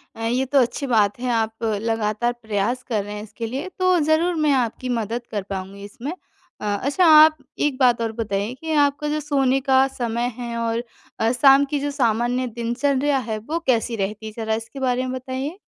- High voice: Yes, high, 245 Hz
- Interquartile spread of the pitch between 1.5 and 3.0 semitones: No, average, 3.8 semitones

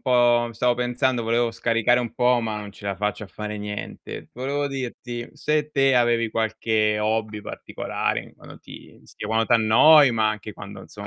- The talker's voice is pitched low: Yes, low, 115 Hz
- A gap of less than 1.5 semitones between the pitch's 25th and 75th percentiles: No, narrow, 2.5 semitones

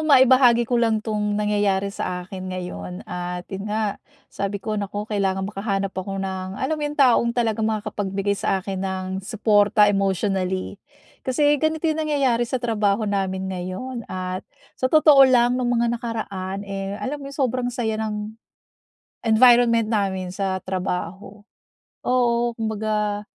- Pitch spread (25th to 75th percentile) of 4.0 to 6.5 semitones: No, average, 3.6 semitones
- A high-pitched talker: Yes, high, 210 Hz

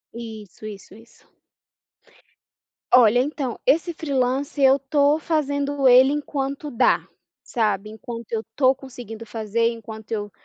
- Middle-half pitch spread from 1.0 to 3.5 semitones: No, average, 4.1 semitones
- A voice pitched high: Yes, very high, 250 Hz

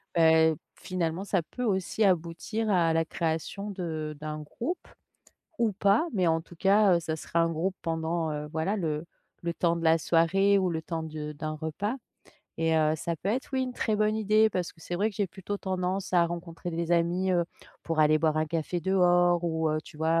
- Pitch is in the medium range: Yes, medium, 170 Hz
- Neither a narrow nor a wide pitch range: Yes, average, 3.1 semitones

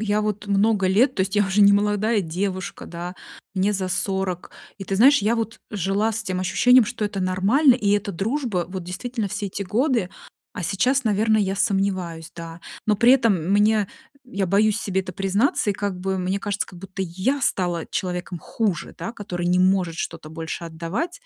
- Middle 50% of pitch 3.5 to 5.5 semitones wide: No, average, 2.8 semitones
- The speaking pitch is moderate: No, high, 195 Hz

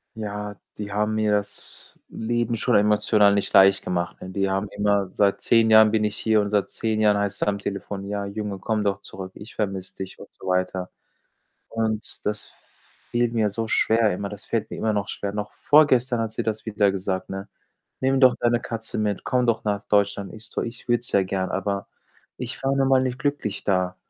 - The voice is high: No, low, 105 Hz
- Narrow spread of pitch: Yes, narrow, 2.2 semitones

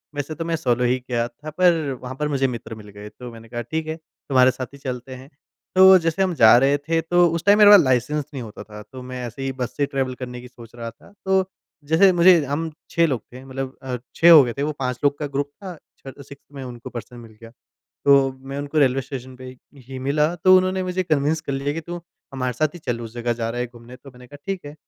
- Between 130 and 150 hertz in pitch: Yes, low, 135 Hz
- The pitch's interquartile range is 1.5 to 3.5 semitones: No, average, 4.2 semitones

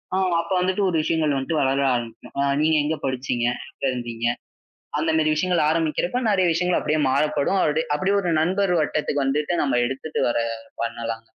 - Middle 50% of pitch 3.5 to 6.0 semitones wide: Yes, average, 4.2 semitones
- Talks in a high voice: No, medium, 155 Hz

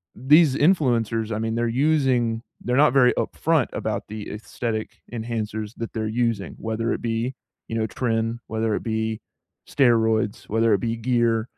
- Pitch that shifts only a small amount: Yes, narrow, 1.8 semitones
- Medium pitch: No, low, 115 Hz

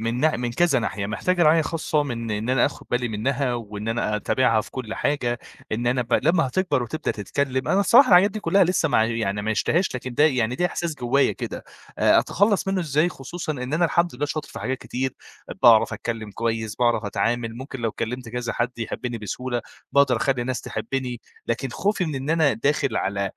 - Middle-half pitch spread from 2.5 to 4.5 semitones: No, average, 5.0 semitones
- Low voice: Yes, low, 125 Hz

